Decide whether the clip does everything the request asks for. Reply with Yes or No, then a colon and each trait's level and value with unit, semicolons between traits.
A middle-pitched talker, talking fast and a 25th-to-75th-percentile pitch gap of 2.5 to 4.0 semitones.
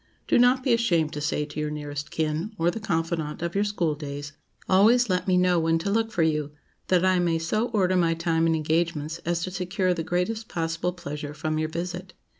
Yes: medium, 170 Hz; fast, 215 wpm; average, 3.0 semitones